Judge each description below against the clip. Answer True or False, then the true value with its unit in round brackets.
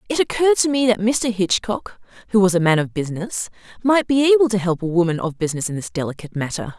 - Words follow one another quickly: True (230 wpm)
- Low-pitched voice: False (205 Hz)